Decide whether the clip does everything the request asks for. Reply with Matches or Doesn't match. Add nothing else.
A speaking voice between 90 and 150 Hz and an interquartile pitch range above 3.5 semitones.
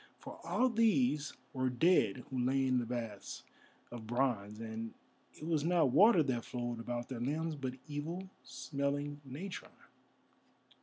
Matches